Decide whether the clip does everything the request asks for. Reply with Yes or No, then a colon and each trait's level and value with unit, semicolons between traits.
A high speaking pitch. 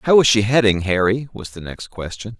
No: low, 105 Hz